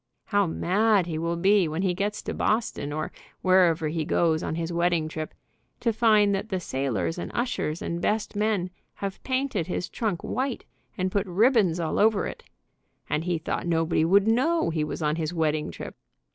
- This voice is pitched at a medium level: Yes, medium, 180 Hz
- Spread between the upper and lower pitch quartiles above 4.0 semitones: Yes, average, 4.4 semitones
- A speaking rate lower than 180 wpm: No, average, 185 wpm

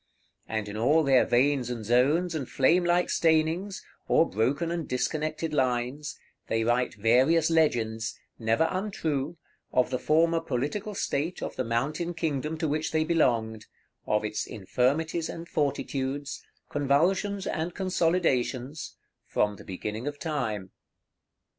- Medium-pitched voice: Yes, medium, 145 Hz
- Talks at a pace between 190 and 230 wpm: No, slow, 135 wpm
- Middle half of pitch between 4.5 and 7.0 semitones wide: Yes, average, 5.1 semitones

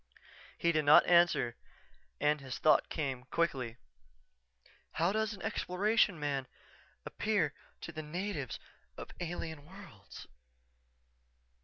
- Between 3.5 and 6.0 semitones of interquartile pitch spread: Yes, average, 4.2 semitones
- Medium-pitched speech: Yes, medium, 160 Hz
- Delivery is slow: Yes, slow, 115 wpm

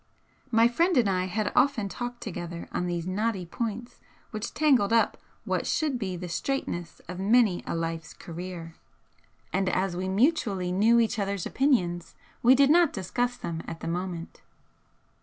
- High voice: Yes, high, 200 Hz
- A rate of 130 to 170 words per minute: Yes, average, 160 wpm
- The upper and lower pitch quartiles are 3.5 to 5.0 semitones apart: No, wide, 5.5 semitones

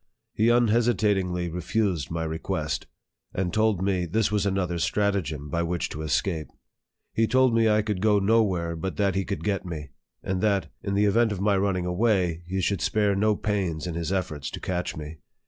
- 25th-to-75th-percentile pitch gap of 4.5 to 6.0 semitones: No, average, 3.4 semitones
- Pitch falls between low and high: No, very low, 95 Hz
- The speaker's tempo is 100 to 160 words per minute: No, average, 190 wpm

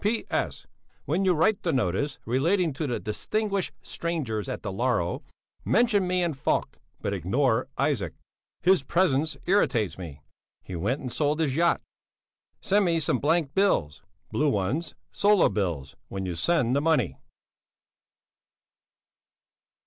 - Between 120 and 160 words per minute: Yes, slow, 135 wpm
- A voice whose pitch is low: No, medium, 145 Hz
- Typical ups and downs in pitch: No, wide, 8.3 semitones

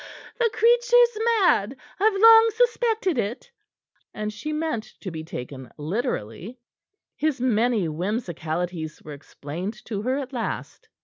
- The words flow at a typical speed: No, slow, 125 wpm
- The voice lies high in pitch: Yes, high, 235 Hz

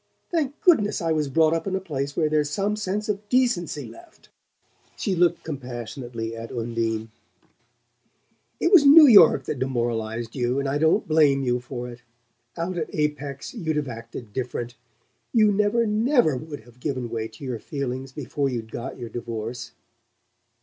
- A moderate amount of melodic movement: No, wide, 7.4 semitones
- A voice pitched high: No, medium, 140 Hz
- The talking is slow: No, average, 165 wpm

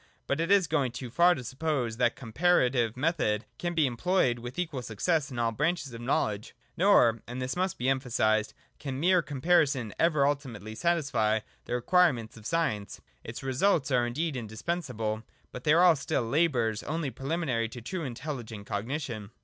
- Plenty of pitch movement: Yes, wide, 5.8 semitones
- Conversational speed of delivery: Yes, average, 180 wpm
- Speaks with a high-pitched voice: No, low, 130 Hz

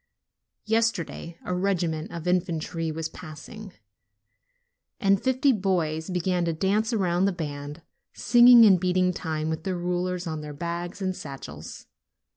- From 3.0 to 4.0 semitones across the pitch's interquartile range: Yes, average, 3.3 semitones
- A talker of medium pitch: Yes, medium, 180 Hz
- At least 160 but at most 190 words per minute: No, average, 140 wpm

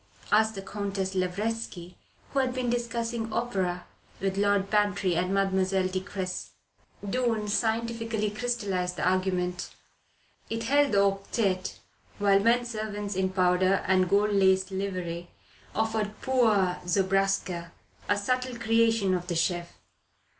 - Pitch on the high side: Yes, high, 200 Hz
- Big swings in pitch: No, average, 3.3 semitones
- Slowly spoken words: Yes, slow, 125 wpm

